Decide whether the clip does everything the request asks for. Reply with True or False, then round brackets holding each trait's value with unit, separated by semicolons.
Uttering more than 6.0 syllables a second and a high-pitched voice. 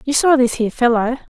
True (6.5 syllables/s; 250 Hz)